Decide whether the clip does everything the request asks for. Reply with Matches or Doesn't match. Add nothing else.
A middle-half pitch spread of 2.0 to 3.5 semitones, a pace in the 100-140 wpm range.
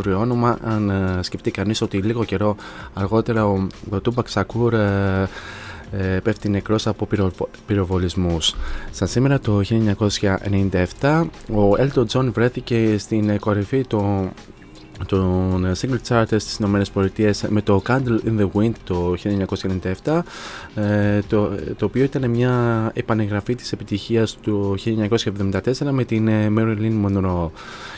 Matches